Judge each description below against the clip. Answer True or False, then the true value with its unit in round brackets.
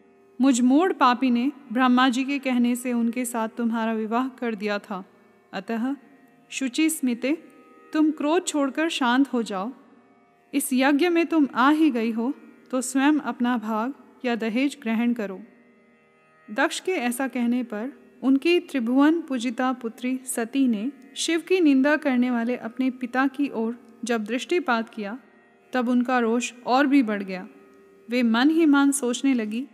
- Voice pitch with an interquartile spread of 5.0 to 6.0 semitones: False (3.0 semitones)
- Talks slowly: False (155 wpm)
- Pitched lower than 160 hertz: False (250 Hz)